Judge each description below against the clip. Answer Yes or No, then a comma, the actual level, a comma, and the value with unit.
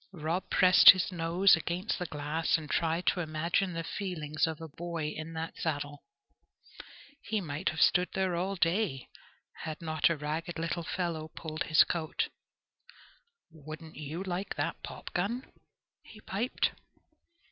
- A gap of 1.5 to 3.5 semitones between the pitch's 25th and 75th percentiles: Yes, narrow, 2.5 semitones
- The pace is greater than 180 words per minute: No, average, 145 wpm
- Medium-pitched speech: Yes, medium, 165 Hz